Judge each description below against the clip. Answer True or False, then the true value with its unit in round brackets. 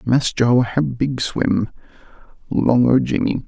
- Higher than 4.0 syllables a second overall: False (3.5 syllables/s)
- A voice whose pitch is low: True (125 Hz)